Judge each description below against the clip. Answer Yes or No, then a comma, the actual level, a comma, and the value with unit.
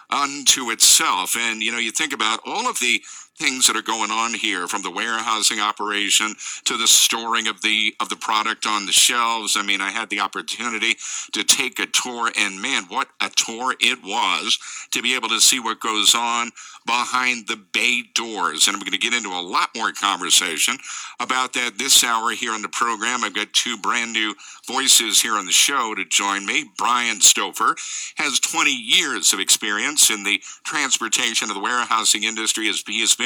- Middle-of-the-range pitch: No, low, 115 Hz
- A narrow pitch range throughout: Yes, narrow, 2.1 semitones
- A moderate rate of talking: Yes, average, 195 wpm